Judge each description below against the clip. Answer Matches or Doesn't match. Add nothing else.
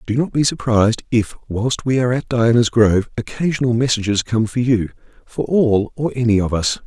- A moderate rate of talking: Matches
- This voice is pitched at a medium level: Doesn't match